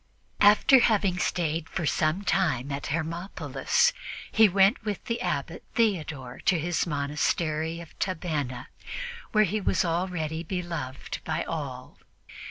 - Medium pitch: Yes, medium, 170 Hz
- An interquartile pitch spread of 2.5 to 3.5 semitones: No, average, 3.9 semitones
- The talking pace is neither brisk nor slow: No, slow, 125 wpm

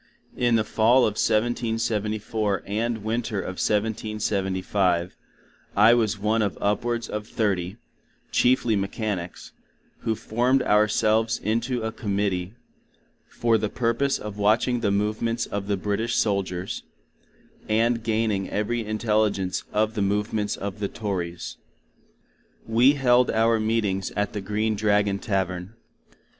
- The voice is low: Yes, low, 105 Hz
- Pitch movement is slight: Yes, narrow, 2.1 semitones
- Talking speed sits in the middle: No, slow, 125 wpm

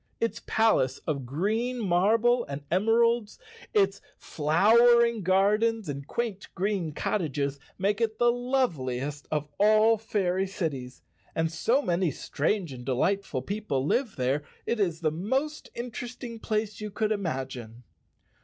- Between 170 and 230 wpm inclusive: No, slow, 135 wpm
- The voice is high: Yes, high, 200 Hz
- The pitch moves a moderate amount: No, wide, 7.2 semitones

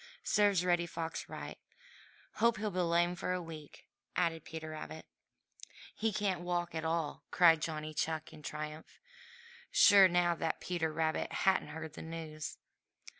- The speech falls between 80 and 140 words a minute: No, average, 150 wpm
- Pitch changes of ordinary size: No, narrow, 2.0 semitones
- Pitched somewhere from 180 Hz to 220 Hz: No, medium, 165 Hz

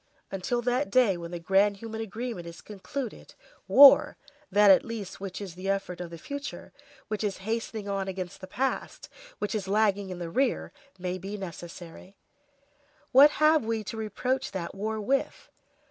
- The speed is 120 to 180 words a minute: Yes, average, 170 wpm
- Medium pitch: No, high, 205 Hz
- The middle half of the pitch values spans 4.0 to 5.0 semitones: No, average, 3.6 semitones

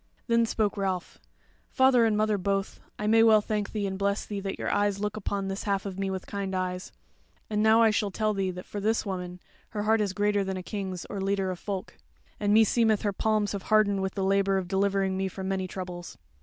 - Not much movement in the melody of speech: Yes, narrow, 1.7 semitones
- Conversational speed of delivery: No, fast, 235 wpm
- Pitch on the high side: Yes, high, 200 Hz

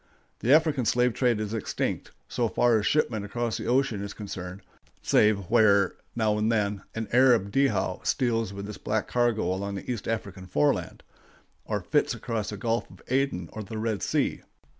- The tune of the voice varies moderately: Yes, average, 3.1 semitones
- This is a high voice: No, low, 110 Hz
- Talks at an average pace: Yes, average, 180 wpm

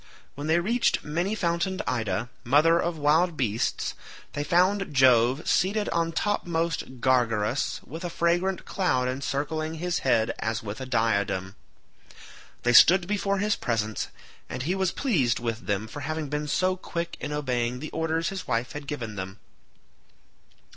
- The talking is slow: No, average, 155 wpm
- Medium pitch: Yes, medium, 150 Hz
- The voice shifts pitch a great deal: Yes, wide, 6.2 semitones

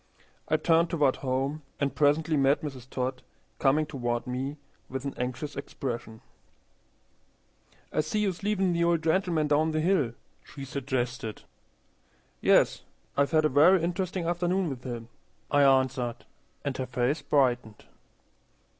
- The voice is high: No, medium, 140 Hz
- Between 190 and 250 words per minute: No, slow, 135 wpm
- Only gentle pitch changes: No, average, 4.0 semitones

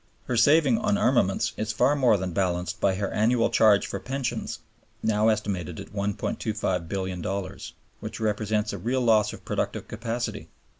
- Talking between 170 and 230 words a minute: No, average, 150 wpm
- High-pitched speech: No, low, 105 Hz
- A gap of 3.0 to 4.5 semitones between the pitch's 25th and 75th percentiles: Yes, average, 3.5 semitones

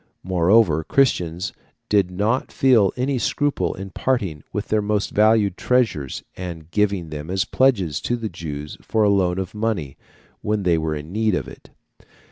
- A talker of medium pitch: No, low, 100 Hz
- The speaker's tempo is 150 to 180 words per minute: Yes, average, 165 wpm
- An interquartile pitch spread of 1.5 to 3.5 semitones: No, average, 4.7 semitones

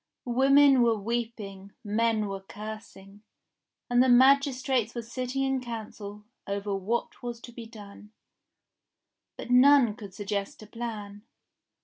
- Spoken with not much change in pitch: No, average, 3.3 semitones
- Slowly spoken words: Yes, slow, 125 wpm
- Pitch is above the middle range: Yes, high, 230 Hz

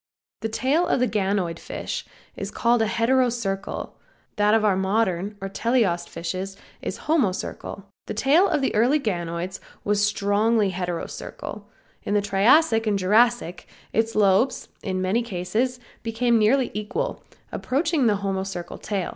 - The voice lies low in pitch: No, high, 210 Hz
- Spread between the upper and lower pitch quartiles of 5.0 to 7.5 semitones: No, average, 3.8 semitones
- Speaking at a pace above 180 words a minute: No, average, 140 wpm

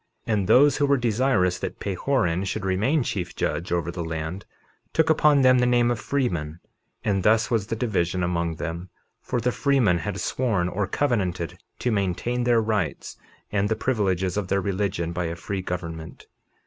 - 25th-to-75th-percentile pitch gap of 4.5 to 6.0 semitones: Yes, wide, 5.5 semitones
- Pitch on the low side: Yes, low, 100 Hz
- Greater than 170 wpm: Yes, average, 180 wpm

